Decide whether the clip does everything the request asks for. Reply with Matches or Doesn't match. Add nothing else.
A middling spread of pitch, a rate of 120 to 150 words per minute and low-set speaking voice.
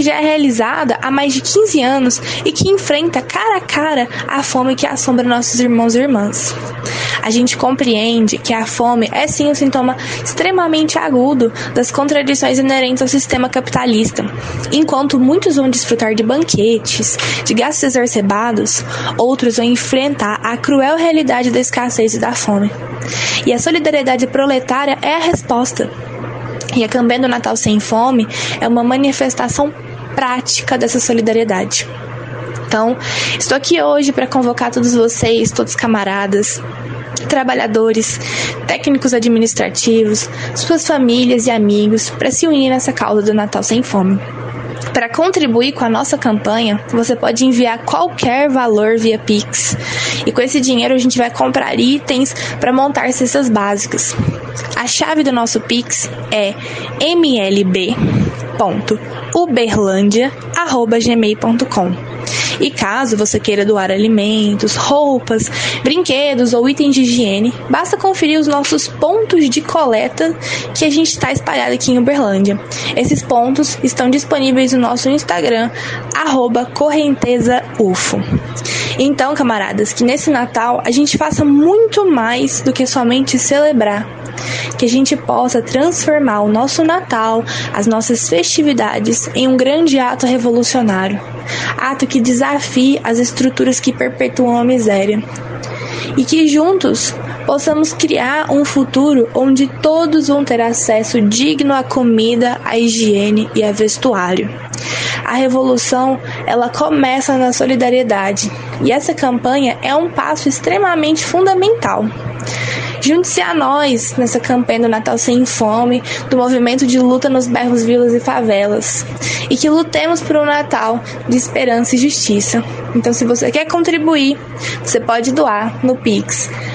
Doesn't match